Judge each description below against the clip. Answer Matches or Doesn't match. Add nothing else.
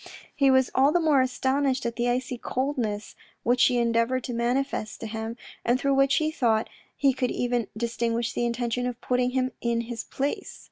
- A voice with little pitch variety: Matches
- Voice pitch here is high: Matches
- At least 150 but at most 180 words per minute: Doesn't match